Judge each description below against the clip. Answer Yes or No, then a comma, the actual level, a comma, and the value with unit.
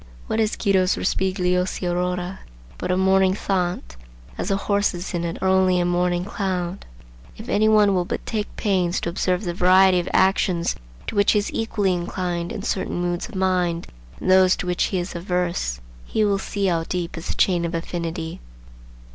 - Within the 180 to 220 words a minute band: Yes, average, 190 wpm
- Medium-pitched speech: Yes, medium, 180 Hz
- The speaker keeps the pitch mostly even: Yes, narrow, 1.6 semitones